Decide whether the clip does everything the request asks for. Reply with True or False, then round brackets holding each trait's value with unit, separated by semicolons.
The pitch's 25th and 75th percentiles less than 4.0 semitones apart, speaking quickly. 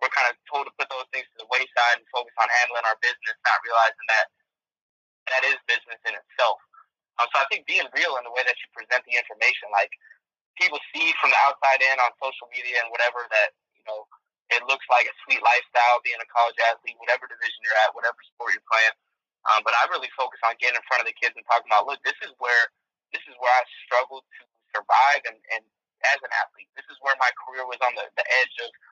True (3.5 semitones; 235 wpm)